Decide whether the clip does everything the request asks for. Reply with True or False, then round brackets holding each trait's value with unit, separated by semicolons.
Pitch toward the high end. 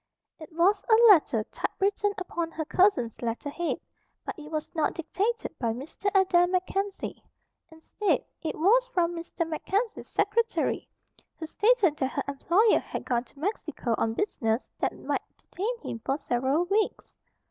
True (340 Hz)